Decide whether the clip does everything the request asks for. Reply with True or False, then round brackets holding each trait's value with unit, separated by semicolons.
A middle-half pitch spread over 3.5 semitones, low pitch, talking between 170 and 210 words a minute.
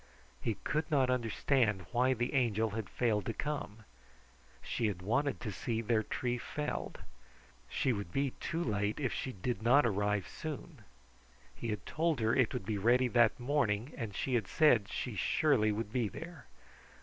True (3.9 semitones; 120 Hz; 175 wpm)